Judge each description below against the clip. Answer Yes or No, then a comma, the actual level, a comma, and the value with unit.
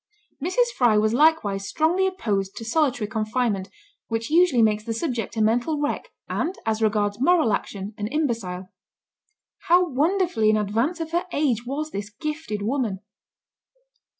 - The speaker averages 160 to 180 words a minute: No, average, 150 wpm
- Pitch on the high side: Yes, high, 235 Hz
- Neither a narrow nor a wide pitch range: No, wide, 6.7 semitones